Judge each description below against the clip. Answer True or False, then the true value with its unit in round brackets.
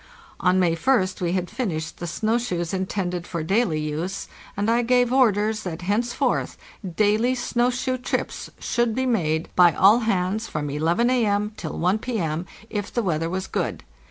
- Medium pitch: False (195 Hz)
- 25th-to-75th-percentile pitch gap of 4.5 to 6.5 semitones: True (5.3 semitones)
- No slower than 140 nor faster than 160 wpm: False (170 wpm)